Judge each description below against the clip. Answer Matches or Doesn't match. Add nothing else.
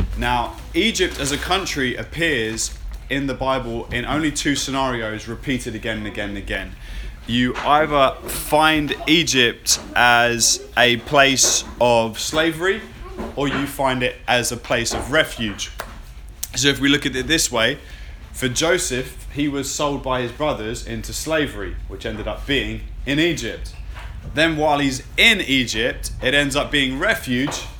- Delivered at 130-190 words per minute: Matches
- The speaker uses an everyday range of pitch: Matches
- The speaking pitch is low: Matches